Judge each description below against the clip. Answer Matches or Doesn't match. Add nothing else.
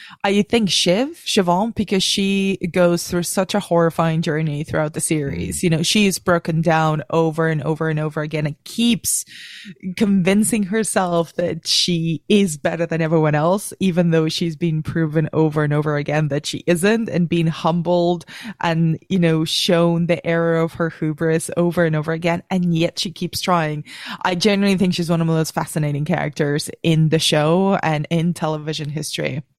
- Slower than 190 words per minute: Matches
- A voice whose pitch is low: Doesn't match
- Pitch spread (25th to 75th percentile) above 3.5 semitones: Doesn't match